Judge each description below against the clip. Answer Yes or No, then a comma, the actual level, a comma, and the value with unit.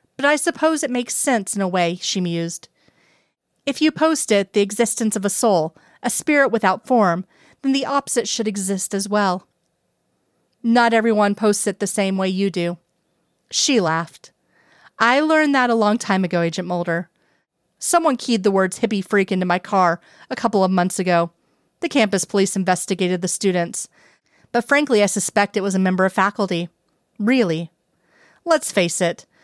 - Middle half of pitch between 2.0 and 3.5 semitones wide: No, average, 4.4 semitones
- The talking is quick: No, average, 175 wpm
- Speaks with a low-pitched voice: No, high, 200 Hz